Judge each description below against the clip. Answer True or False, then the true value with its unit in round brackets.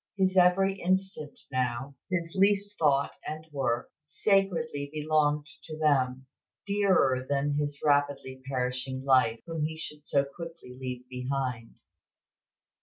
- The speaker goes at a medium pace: False (120 wpm)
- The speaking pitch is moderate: True (145 Hz)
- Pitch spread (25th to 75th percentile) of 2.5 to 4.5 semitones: True (4.2 semitones)